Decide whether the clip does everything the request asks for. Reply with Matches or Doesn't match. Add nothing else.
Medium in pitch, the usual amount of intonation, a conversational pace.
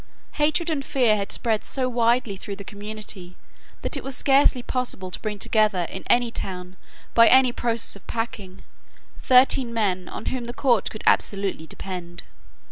Doesn't match